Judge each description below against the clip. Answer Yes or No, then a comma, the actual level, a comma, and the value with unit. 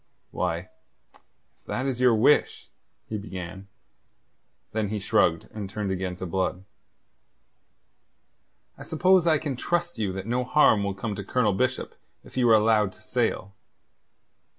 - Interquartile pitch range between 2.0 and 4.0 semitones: No, average, 4.8 semitones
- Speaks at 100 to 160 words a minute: Yes, average, 150 wpm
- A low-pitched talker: Yes, low, 105 Hz